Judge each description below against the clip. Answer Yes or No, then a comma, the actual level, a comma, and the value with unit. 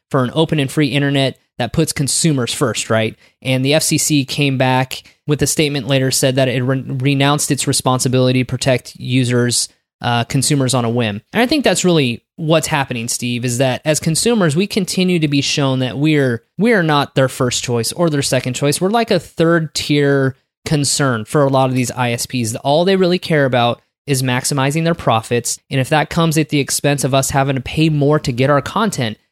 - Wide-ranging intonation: No, average, 3.3 semitones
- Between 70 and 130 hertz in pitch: No, medium, 140 Hz